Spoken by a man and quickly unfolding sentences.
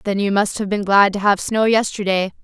No: female; fast, 245 wpm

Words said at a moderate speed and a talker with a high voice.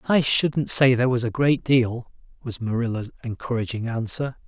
No: average, 160 wpm; low, 125 Hz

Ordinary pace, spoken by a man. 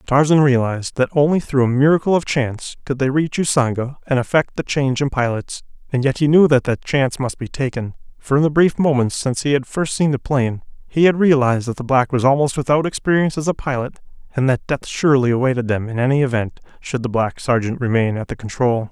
No: fast, 225 wpm; male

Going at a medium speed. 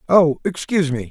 Yes: average, 160 wpm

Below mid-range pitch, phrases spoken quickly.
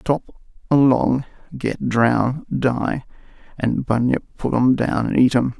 No: low, 125 Hz; average, 140 wpm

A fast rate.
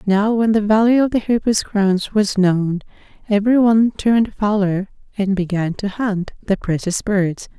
No: average, 165 wpm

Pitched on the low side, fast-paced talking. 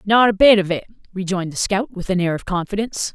No: high, 195 Hz; fast, 250 wpm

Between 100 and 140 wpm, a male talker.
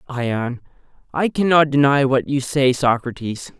Yes: slow, 135 wpm; male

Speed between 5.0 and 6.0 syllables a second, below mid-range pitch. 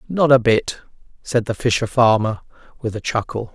Yes: 5.1 syllables/s; low, 115 Hz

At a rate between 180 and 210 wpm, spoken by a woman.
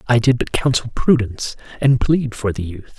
No: average, 200 wpm; male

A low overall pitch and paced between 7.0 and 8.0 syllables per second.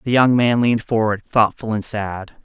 No: low, 110 Hz; 4.9 syllables/s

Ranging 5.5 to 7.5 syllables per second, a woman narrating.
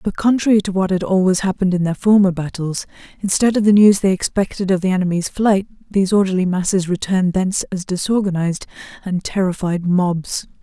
Yes: 6.0 syllables/s; female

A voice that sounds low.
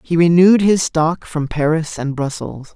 No: medium, 160 Hz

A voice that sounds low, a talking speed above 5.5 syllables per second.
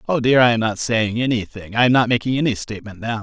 Yes: low, 115 Hz; 6.5 syllables/s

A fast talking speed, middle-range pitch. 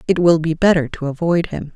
Yes: fast, 240 wpm; medium, 165 Hz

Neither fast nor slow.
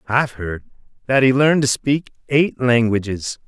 Yes: average, 155 wpm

